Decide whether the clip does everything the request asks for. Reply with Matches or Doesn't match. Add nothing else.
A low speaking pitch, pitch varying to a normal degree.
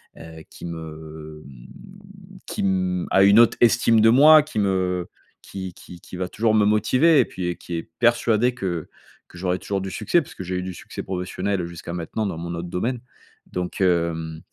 Matches